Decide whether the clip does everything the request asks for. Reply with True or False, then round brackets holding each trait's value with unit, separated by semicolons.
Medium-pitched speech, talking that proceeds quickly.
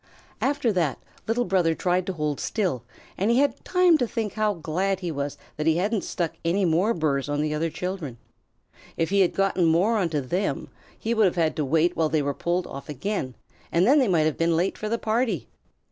True (175 Hz; 220 wpm)